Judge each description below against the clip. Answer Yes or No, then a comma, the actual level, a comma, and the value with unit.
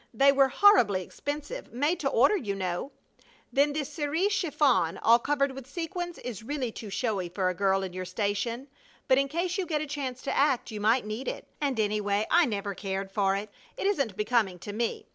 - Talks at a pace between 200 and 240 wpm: Yes, fast, 205 wpm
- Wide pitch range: Yes, wide, 6.2 semitones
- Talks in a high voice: Yes, very high, 250 Hz